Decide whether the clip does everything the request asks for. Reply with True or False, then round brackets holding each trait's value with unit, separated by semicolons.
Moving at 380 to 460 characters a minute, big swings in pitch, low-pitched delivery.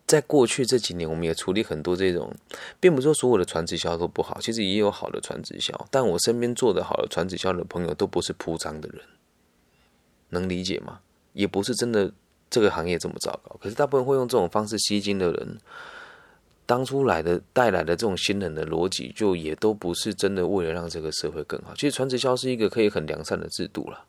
False (340 characters per minute; 6.4 semitones; 100 Hz)